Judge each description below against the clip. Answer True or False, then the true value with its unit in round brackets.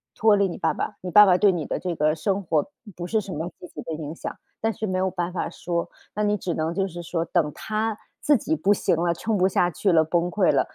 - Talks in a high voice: False (180 Hz)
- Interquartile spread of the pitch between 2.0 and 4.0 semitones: True (3.4 semitones)